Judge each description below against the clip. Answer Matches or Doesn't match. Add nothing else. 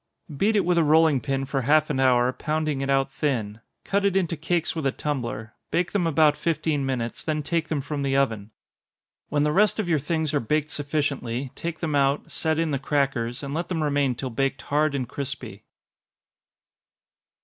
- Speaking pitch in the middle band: Matches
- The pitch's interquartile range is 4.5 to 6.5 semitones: Doesn't match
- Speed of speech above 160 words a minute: Matches